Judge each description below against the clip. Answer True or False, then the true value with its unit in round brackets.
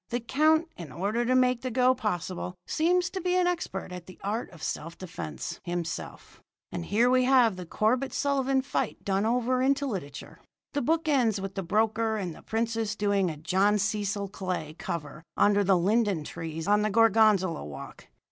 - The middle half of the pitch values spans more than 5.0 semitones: True (5.5 semitones)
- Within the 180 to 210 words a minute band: True (185 wpm)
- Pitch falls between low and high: False (210 Hz)